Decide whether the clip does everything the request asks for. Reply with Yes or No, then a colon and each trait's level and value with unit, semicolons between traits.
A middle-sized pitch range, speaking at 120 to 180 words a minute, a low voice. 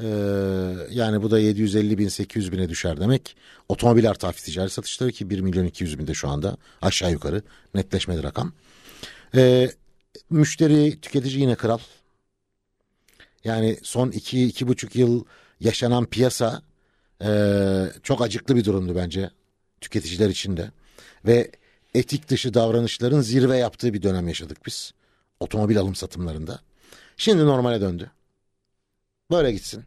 Yes: average, 4.3 semitones; average, 130 wpm; low, 105 Hz